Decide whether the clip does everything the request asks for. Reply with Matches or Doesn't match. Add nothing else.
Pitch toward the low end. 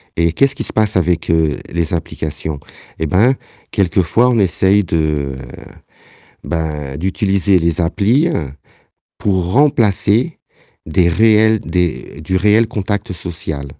Matches